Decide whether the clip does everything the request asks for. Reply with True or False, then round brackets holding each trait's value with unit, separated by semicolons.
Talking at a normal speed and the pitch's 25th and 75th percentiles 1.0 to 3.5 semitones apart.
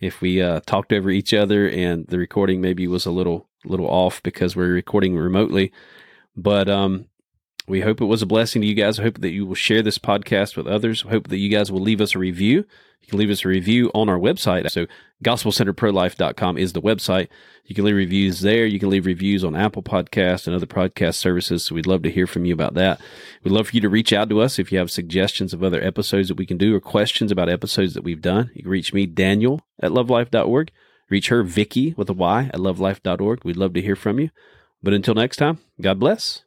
False (235 wpm; 2.6 semitones)